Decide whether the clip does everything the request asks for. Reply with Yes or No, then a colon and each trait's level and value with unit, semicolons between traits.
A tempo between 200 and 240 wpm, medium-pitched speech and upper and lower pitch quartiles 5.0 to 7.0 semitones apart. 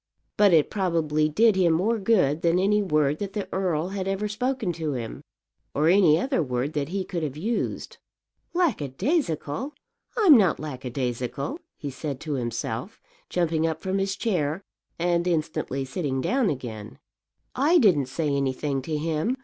No: average, 155 wpm; medium, 165 Hz; wide, 5.6 semitones